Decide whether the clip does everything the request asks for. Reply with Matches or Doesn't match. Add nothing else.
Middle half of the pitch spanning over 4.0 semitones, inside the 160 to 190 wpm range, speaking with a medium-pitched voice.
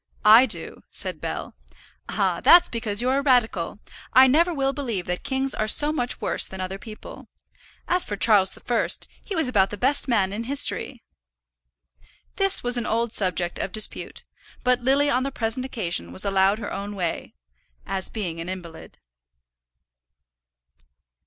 Doesn't match